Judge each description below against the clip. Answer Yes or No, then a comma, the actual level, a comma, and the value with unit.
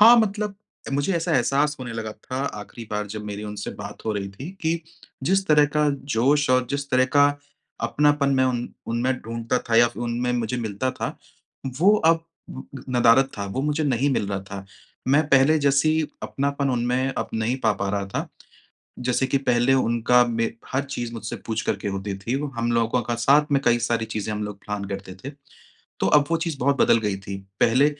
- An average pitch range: Yes, average, 4.1 semitones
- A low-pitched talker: Yes, low, 125 Hz